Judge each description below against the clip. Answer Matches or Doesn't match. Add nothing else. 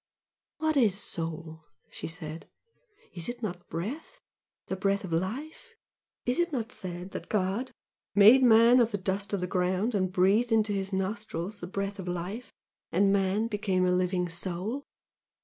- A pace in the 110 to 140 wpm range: Doesn't match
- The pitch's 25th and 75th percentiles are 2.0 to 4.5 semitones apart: Matches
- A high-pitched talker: Matches